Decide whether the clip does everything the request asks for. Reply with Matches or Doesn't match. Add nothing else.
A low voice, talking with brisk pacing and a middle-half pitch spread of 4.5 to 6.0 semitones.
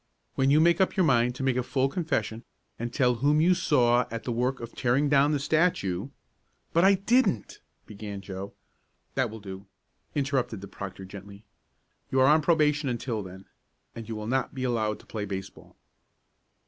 Doesn't match